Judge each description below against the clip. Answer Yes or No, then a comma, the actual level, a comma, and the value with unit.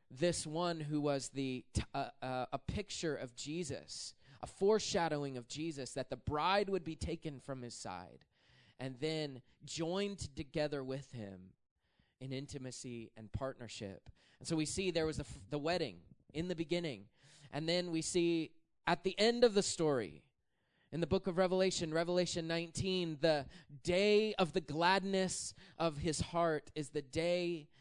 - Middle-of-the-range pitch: Yes, medium, 155 Hz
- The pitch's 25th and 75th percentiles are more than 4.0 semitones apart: Yes, average, 4.6 semitones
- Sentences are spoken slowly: No, average, 165 wpm